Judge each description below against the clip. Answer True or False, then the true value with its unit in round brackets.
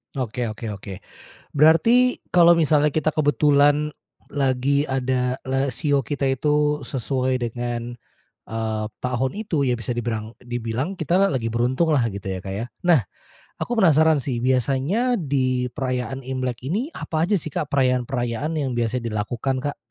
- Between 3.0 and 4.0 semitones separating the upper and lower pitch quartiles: True (3.7 semitones)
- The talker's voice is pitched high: False (130 Hz)